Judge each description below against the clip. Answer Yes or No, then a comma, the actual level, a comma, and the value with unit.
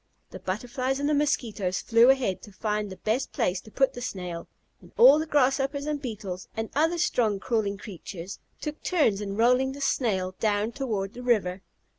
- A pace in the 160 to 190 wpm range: Yes, average, 185 wpm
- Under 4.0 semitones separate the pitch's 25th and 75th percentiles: No, average, 5.3 semitones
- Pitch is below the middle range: No, high, 230 Hz